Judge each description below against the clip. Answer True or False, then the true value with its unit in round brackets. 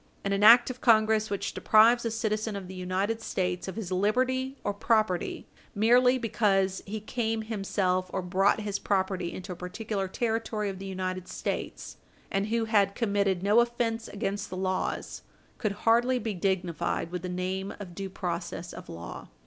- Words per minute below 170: False (175 wpm)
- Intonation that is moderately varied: True (3.2 semitones)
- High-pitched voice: True (200 Hz)